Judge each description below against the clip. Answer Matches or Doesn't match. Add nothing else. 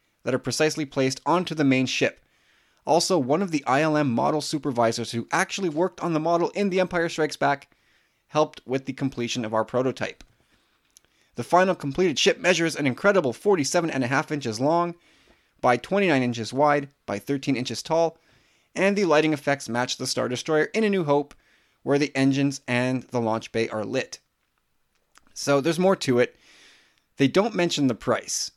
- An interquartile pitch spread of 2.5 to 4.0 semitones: Doesn't match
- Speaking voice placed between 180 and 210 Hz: Doesn't match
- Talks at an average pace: Matches